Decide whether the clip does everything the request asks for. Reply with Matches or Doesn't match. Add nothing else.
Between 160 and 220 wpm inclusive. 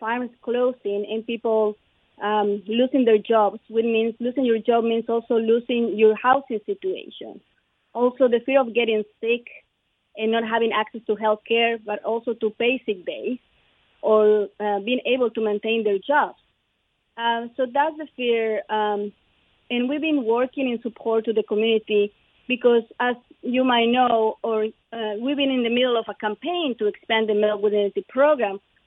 Matches